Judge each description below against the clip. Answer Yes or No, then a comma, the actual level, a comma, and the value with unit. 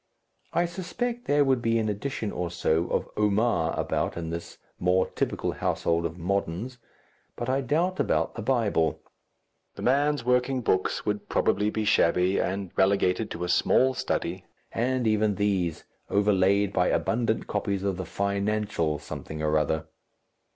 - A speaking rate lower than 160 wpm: Yes, average, 150 wpm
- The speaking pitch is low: Yes, low, 105 Hz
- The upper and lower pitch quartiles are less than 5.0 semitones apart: No, average, 5.3 semitones